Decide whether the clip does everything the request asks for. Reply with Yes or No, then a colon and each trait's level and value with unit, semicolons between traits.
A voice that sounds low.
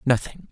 Yes: low, 125 Hz